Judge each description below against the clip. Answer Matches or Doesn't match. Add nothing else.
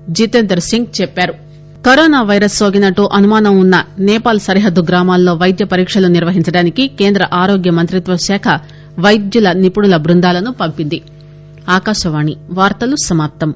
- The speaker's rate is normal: Doesn't match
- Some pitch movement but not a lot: Matches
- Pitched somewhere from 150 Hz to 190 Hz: Matches